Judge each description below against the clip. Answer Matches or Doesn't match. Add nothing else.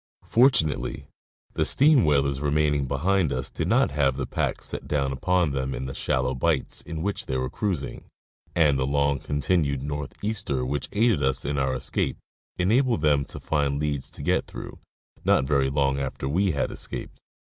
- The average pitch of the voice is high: Doesn't match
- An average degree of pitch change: Matches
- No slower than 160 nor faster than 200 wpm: Matches